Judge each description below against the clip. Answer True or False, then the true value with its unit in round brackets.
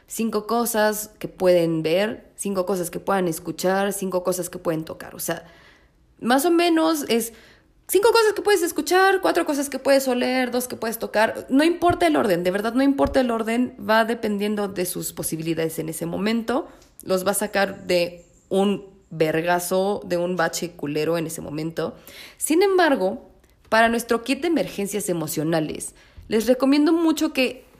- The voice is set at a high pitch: True (205 Hz)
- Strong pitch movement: True (7.1 semitones)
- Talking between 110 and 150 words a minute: False (170 wpm)